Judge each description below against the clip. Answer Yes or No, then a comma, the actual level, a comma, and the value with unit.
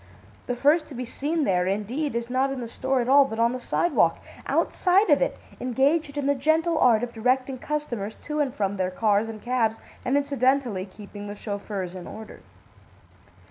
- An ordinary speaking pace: Yes, average, 190 wpm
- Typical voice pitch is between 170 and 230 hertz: No, very high, 250 Hz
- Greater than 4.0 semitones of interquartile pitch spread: Yes, average, 4.7 semitones